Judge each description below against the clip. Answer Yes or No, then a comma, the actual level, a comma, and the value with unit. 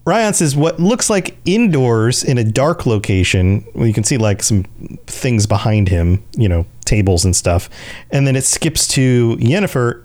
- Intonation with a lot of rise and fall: Yes, wide, 5.8 semitones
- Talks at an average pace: Yes, average, 185 wpm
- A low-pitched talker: Yes, low, 115 Hz